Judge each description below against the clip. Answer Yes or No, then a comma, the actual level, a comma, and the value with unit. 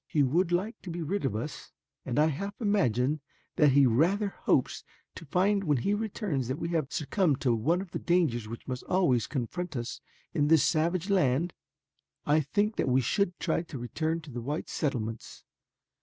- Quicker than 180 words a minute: Yes, average, 190 wpm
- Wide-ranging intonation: Yes, wide, 5.8 semitones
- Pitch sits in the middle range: Yes, medium, 155 Hz